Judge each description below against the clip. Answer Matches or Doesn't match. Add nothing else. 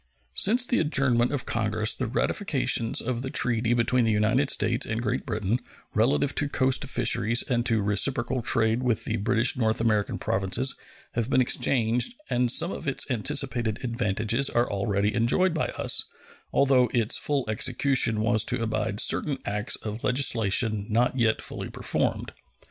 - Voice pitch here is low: Matches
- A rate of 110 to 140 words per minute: Doesn't match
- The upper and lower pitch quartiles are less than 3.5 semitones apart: Matches